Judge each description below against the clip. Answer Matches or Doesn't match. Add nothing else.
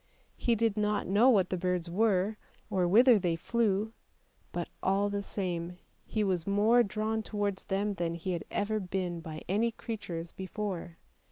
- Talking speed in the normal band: Matches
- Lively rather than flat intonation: Doesn't match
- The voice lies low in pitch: Doesn't match